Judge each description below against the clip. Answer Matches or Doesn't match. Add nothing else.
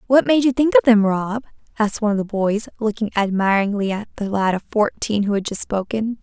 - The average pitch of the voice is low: Doesn't match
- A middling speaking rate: Doesn't match